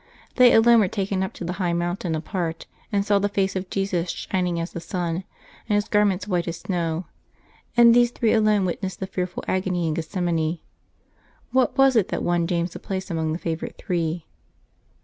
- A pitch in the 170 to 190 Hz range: Yes, medium, 185 Hz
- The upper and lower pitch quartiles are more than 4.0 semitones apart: No, average, 3.0 semitones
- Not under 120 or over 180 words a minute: No, average, 195 wpm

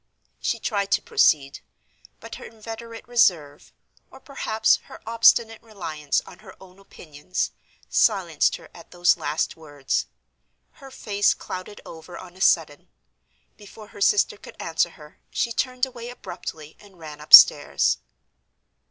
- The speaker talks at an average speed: No, slow, 130 wpm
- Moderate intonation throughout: No, wide, 5.8 semitones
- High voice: Yes, high, 195 Hz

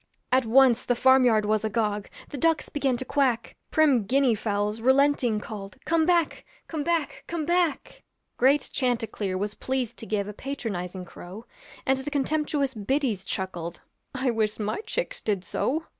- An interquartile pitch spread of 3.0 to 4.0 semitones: No, average, 5.0 semitones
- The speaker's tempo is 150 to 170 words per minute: Yes, average, 160 wpm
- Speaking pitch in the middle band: No, high, 245 Hz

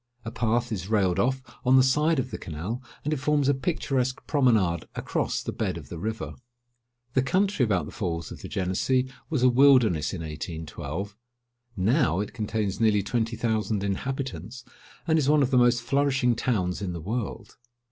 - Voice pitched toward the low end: Yes, low, 115 Hz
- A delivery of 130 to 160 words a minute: No, average, 180 wpm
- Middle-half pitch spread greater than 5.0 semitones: Yes, wide, 5.4 semitones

